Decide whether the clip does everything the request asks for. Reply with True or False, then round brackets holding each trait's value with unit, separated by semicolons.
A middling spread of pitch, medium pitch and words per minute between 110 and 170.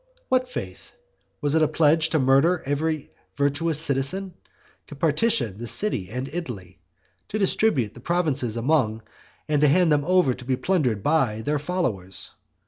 True (4.8 semitones; 145 Hz; 155 wpm)